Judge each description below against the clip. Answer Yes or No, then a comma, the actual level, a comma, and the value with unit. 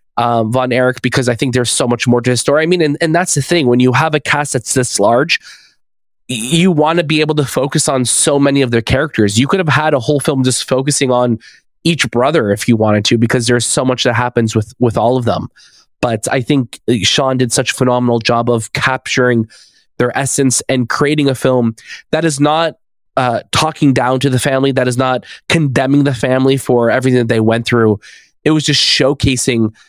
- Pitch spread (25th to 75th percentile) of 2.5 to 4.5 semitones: Yes, average, 3.1 semitones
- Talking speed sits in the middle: No, fast, 220 wpm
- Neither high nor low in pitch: No, low, 130 Hz